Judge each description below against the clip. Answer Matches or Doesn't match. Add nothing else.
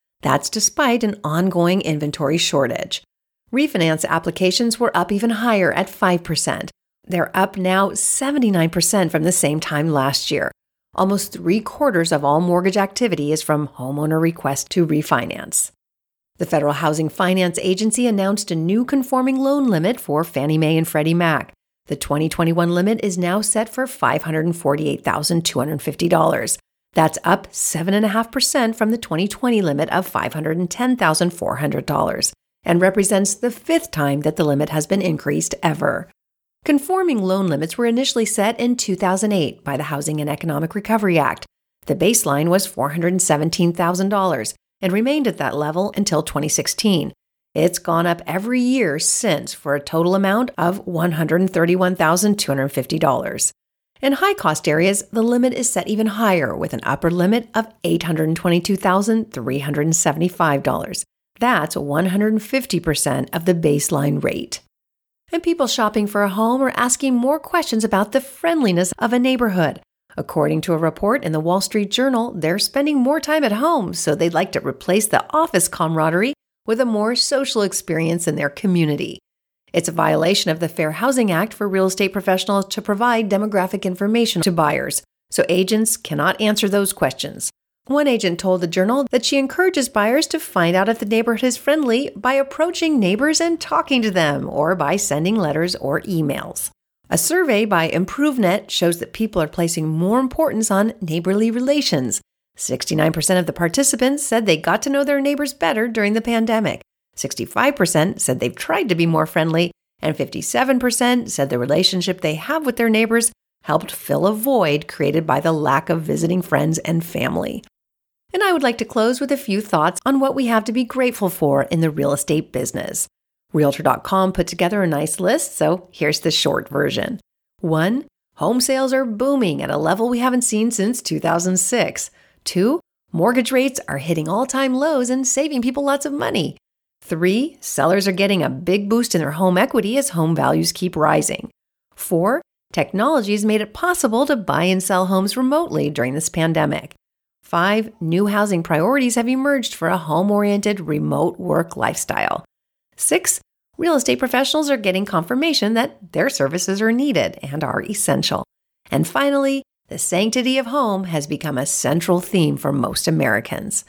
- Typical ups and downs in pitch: Doesn't match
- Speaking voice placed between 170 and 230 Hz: Matches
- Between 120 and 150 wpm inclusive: Doesn't match